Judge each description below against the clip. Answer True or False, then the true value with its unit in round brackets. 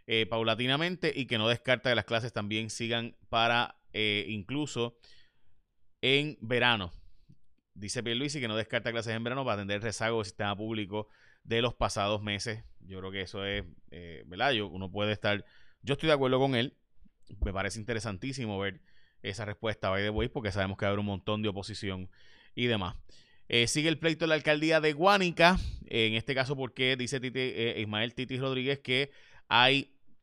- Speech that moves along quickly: True (195 wpm)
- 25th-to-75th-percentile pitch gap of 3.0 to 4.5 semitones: True (4.0 semitones)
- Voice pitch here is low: True (115 Hz)